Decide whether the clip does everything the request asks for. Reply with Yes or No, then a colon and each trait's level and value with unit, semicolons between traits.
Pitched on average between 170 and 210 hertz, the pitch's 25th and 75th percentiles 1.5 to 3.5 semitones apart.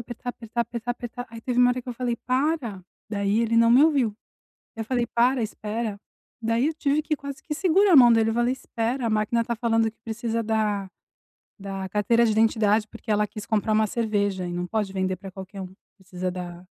No: high, 225 Hz; average, 2.8 semitones